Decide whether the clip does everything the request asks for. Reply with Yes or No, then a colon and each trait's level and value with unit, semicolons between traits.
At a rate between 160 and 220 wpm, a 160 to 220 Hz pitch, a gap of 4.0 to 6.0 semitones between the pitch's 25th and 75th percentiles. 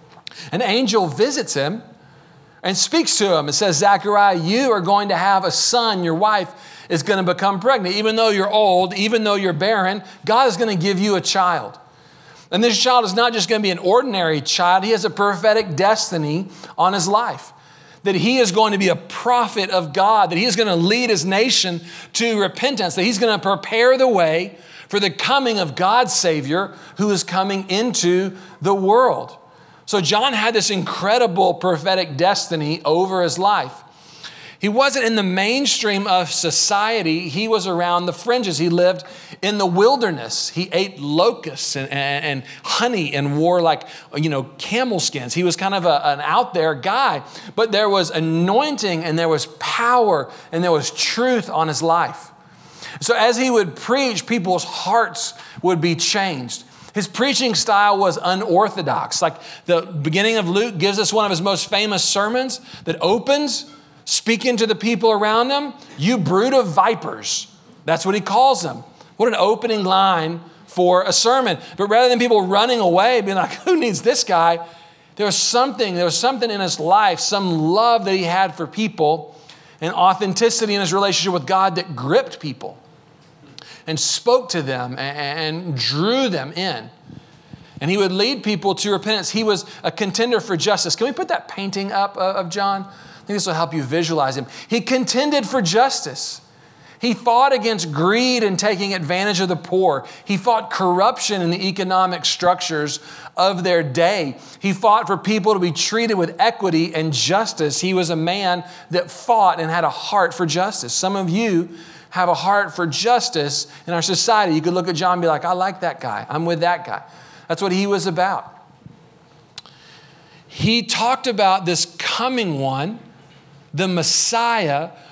Yes: average, 180 wpm; high, 190 Hz; average, 4.5 semitones